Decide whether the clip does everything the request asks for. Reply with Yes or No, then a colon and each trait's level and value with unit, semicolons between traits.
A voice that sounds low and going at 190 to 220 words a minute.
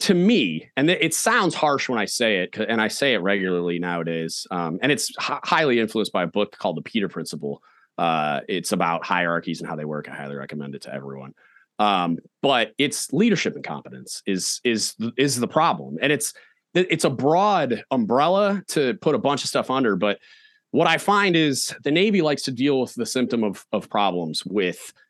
Yes: low, 115 Hz; average, 200 wpm